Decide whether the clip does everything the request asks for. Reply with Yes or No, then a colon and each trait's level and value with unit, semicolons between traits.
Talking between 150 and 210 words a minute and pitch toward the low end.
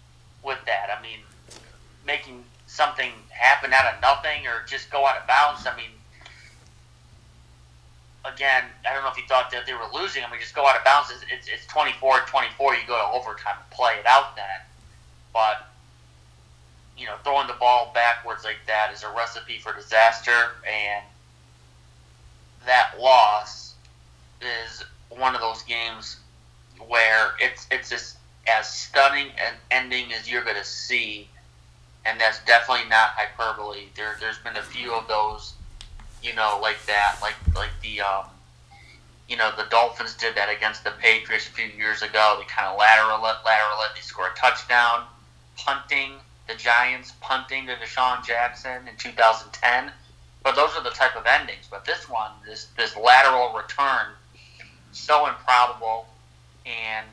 Yes: average, 160 wpm; low, 110 Hz